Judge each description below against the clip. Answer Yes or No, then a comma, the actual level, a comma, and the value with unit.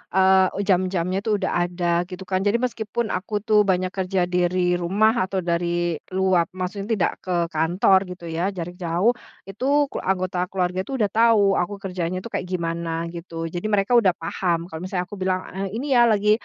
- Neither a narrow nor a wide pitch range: No, narrow, 2.3 semitones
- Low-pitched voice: No, medium, 185 Hz